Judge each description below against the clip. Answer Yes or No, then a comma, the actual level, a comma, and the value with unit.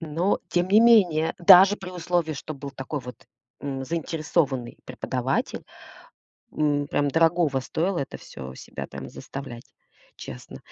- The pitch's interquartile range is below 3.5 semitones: No, average, 4.4 semitones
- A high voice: No, medium, 155 Hz